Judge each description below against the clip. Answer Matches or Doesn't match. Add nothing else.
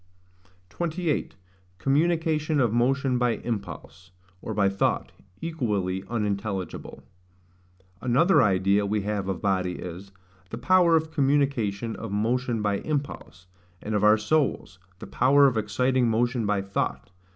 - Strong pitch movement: Matches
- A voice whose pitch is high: Doesn't match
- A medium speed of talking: Doesn't match